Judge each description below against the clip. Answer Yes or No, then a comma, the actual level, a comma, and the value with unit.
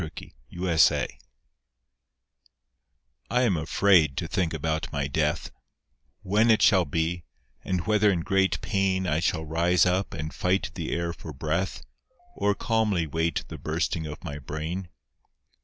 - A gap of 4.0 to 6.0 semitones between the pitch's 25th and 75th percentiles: No, average, 3.4 semitones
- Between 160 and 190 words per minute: No, average, 145 wpm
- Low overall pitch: Yes, very low, 85 Hz